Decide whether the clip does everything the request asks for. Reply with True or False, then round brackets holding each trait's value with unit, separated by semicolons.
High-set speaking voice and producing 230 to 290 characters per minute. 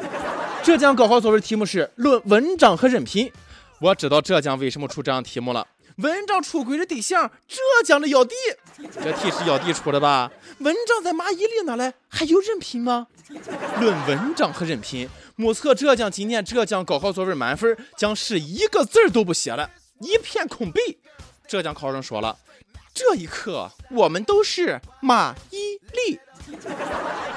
True (240 Hz; 245 characters per minute)